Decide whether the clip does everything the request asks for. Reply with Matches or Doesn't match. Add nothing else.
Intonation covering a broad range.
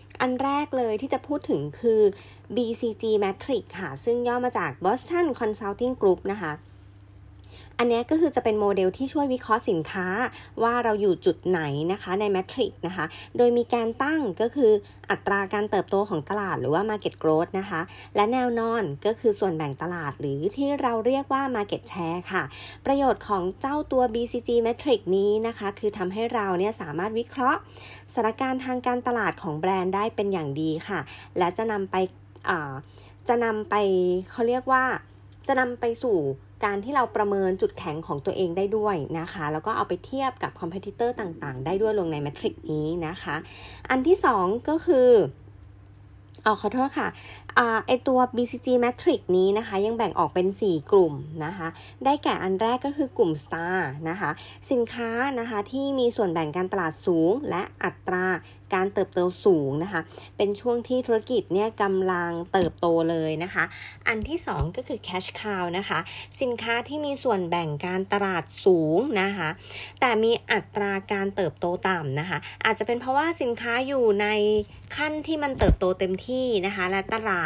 Matches